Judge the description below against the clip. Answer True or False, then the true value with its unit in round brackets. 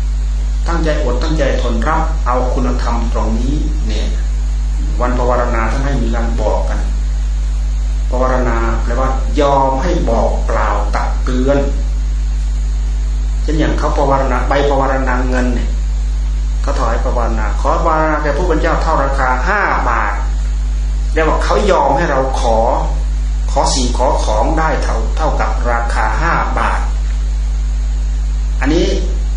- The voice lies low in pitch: True (75 Hz)